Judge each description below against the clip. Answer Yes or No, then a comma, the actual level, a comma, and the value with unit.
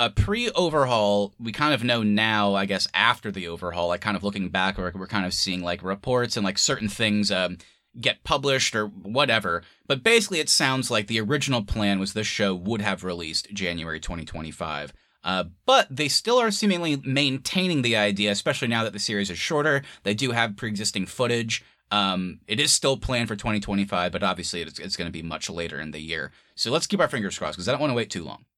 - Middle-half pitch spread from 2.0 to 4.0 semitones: No, average, 5.0 semitones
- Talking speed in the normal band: No, fast, 220 wpm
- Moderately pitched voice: No, low, 105 Hz